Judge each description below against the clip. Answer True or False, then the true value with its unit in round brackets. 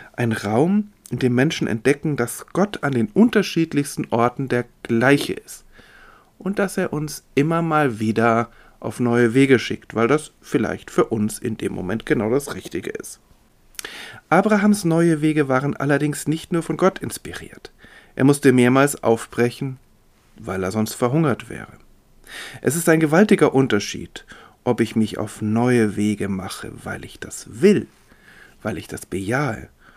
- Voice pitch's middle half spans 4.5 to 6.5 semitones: True (5.6 semitones)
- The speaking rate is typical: True (155 wpm)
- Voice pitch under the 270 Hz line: True (135 Hz)